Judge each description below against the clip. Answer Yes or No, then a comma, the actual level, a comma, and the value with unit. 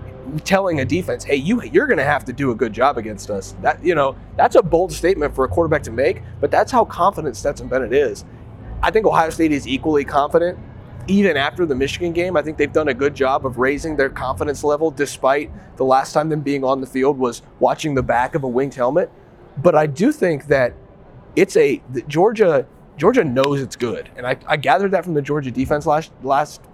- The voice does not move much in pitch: No, average, 3.8 semitones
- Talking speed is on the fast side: Yes, fast, 225 wpm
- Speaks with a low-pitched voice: No, medium, 145 Hz